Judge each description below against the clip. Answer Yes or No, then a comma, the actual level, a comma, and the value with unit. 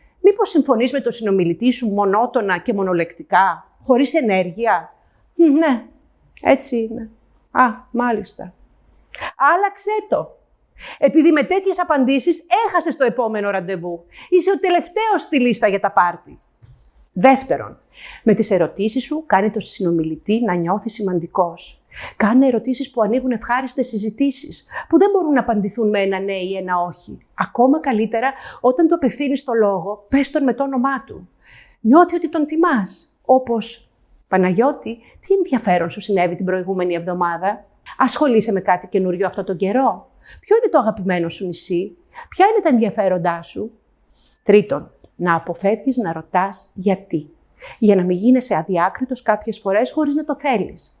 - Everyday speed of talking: Yes, average, 145 wpm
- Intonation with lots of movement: Yes, wide, 6.2 semitones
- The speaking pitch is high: Yes, high, 230 Hz